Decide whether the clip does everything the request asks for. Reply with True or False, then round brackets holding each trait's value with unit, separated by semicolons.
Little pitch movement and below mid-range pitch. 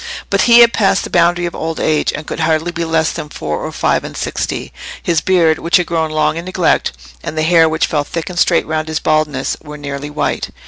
False (1.9 semitones; 160 Hz)